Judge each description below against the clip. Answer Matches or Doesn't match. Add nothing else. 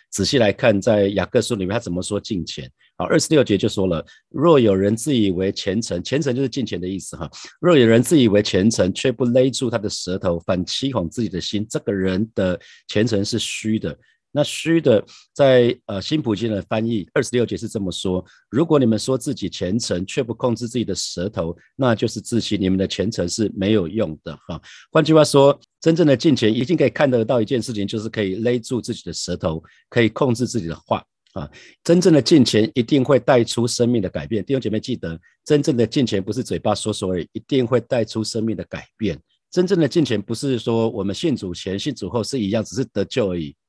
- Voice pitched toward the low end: Matches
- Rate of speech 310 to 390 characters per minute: Matches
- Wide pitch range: Doesn't match